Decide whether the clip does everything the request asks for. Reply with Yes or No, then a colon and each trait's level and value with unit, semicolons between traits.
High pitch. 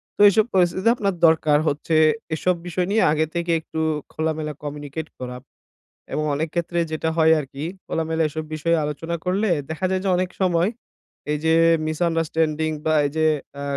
No: medium, 160 Hz